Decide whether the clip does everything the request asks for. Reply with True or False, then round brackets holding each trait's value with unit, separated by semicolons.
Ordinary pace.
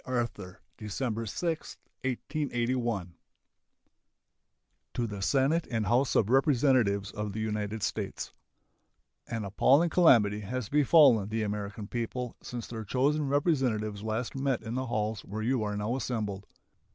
False (130 wpm)